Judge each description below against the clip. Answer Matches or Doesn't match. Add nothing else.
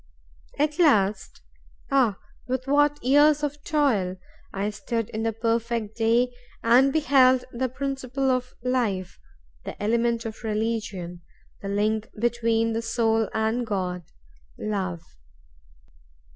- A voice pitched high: Matches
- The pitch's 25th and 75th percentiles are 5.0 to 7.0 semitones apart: Doesn't match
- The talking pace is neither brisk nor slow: Doesn't match